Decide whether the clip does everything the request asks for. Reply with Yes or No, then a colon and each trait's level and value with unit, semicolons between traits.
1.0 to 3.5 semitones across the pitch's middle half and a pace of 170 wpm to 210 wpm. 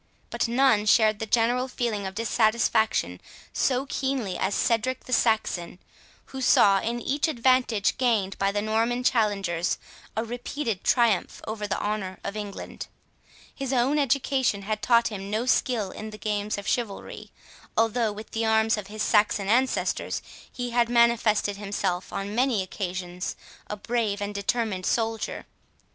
No: average, 3.0 semitones; average, 150 wpm